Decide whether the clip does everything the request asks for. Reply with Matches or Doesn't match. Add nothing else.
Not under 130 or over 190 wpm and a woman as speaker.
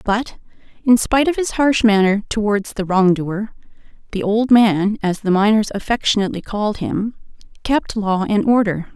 Matches